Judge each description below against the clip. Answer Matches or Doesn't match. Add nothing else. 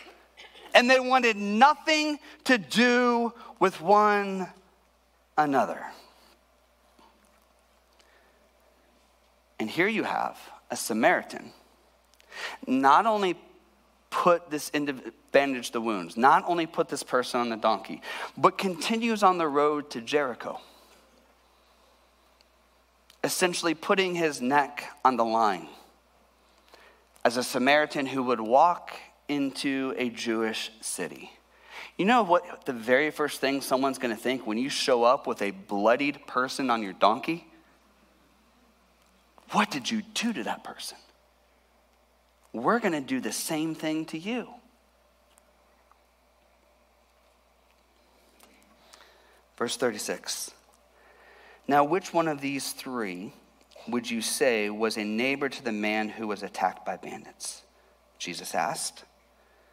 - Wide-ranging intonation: Matches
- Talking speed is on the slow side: Matches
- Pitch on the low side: Doesn't match